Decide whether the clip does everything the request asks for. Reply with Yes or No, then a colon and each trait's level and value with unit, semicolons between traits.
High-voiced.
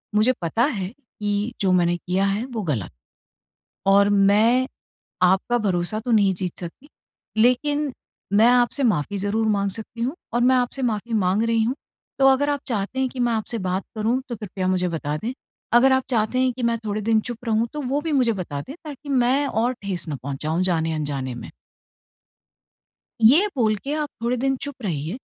Yes: high, 220 Hz